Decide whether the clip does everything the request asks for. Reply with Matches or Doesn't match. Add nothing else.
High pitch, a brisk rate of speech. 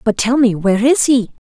Matches